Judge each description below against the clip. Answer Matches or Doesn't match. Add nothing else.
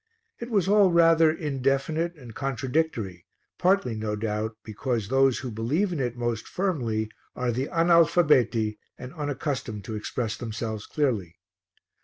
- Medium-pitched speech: Doesn't match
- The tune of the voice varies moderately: Doesn't match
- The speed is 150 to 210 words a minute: Doesn't match